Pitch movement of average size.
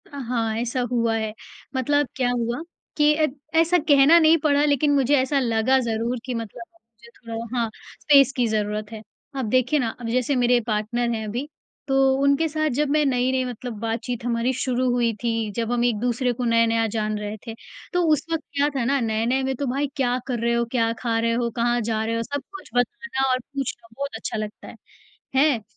Yes: average, 3.1 semitones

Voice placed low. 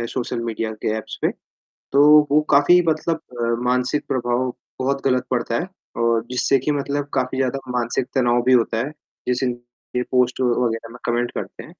Yes: low, 125 Hz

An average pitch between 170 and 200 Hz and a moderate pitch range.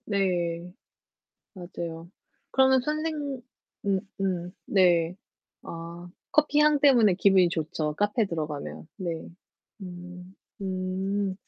Yes: medium, 185 Hz; average, 3.2 semitones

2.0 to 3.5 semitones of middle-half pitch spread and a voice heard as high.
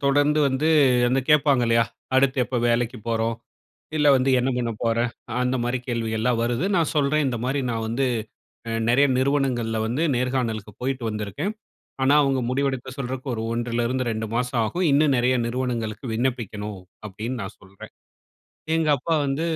No: average, 2.9 semitones; low, 125 Hz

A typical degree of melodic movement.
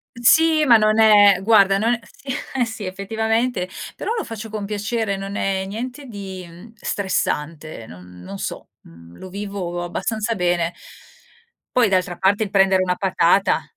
Yes: average, 3.6 semitones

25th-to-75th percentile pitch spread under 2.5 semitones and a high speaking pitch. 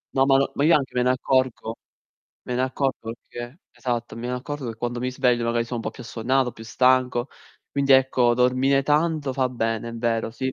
No: narrow, 2.1 semitones; low, 125 Hz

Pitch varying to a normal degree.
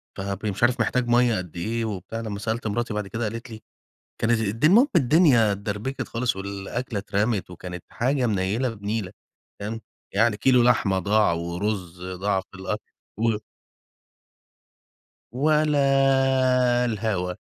Yes: average, 3.4 semitones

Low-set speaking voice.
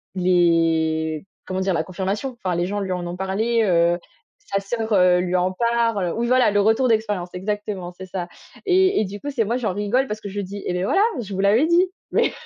No: high, 195 Hz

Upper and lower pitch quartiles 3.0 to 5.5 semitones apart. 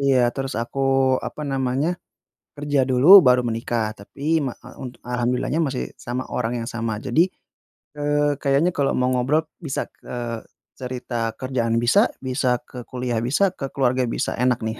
No: narrow, 2.5 semitones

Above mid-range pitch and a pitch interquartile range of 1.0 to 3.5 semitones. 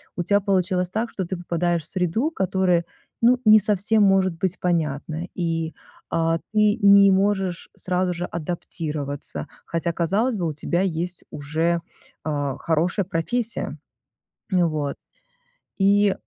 No: medium, 180 Hz; average, 3.2 semitones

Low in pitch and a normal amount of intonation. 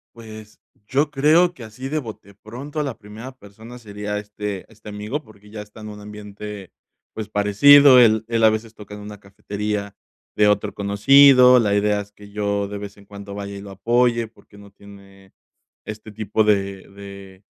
No: low, 105 Hz; narrow, 2.0 semitones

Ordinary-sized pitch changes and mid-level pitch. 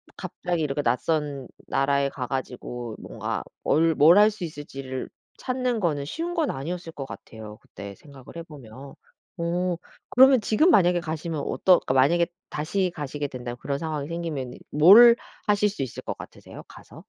Yes: average, 4.8 semitones; medium, 150 Hz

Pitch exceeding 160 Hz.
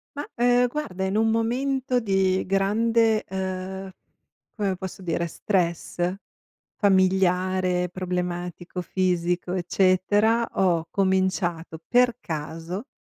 Yes: high, 190 Hz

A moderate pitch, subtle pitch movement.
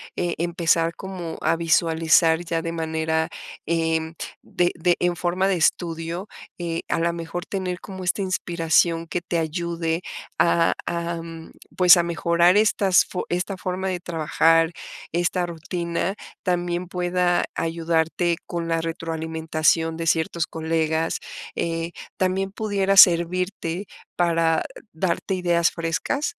Yes: medium, 170 Hz; narrow, 1.5 semitones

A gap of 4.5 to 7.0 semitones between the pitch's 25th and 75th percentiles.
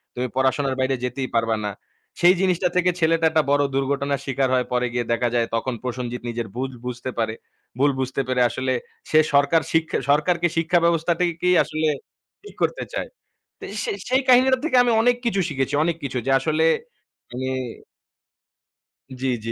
Yes: average, 5.0 semitones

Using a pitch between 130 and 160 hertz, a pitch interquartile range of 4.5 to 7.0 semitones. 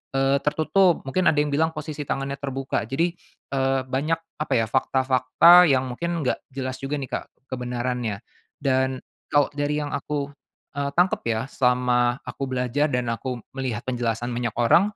No: low, 135 Hz; average, 2.9 semitones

